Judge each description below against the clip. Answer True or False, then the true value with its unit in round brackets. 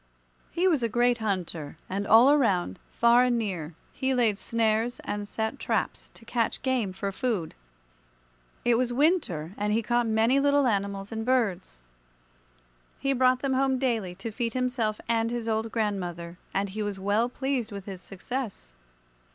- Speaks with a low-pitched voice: False (225 Hz)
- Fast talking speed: False (165 wpm)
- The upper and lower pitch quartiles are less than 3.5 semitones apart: False (4.0 semitones)